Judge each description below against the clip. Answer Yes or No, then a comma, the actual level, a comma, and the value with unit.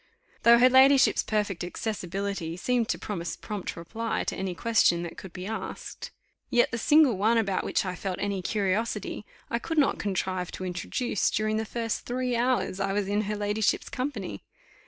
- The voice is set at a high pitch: Yes, high, 210 Hz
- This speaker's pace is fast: No, average, 180 wpm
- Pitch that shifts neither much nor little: Yes, average, 3.8 semitones